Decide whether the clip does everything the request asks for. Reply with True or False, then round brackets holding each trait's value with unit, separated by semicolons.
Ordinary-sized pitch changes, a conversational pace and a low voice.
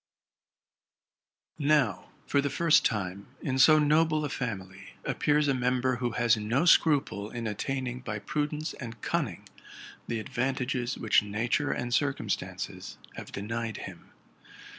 False (4.6 semitones; 130 wpm; 125 Hz)